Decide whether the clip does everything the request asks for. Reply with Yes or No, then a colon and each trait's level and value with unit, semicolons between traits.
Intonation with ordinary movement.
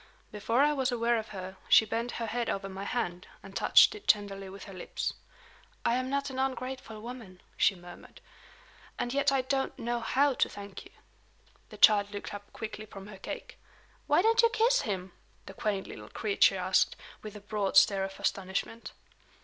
Yes: average, 4.6 semitones